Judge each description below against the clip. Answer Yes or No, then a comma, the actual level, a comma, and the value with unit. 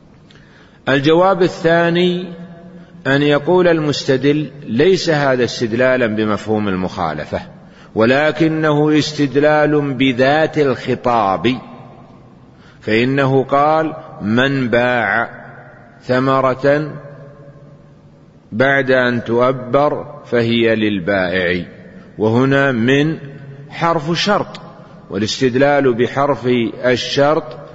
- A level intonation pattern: No, average, 3.8 semitones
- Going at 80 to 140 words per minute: No, slow, 65 wpm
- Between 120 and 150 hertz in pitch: Yes, medium, 140 Hz